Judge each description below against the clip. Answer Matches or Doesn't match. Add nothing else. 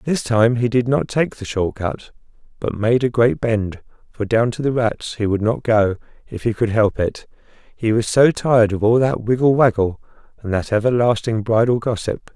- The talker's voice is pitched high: Doesn't match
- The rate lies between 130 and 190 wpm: Doesn't match